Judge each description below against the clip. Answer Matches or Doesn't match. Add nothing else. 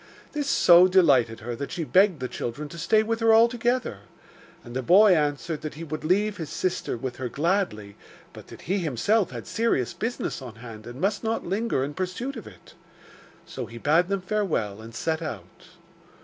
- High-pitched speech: Doesn't match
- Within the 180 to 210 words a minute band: Matches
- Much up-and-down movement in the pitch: Matches